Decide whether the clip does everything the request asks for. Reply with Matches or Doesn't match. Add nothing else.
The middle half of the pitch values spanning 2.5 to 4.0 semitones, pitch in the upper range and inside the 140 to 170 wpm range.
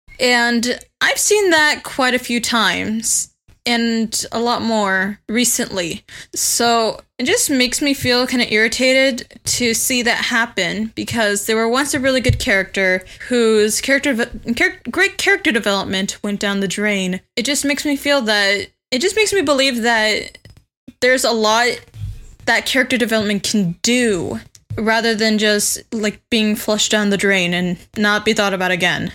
Matches